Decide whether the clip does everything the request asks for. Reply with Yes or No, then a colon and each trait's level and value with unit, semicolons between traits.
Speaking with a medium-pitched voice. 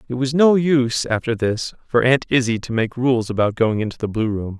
No: low, 120 Hz